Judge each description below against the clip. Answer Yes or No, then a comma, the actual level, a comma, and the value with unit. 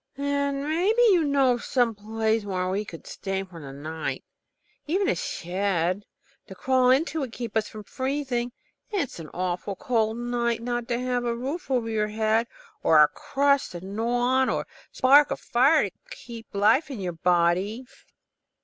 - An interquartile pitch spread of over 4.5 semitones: Yes, average, 5.0 semitones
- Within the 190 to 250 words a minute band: No, average, 175 wpm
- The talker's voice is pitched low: No, high, 235 Hz